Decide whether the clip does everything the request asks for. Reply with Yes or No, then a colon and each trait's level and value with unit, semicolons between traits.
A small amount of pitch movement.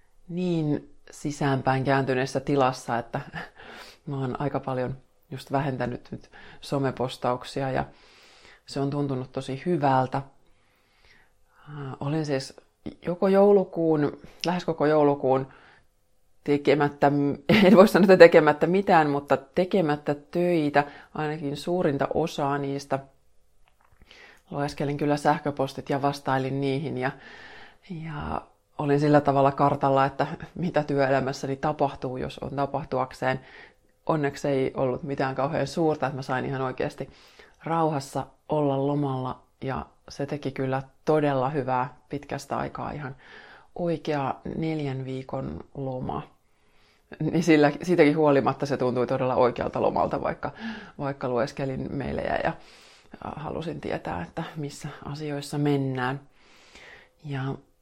Yes: narrow, 2.2 semitones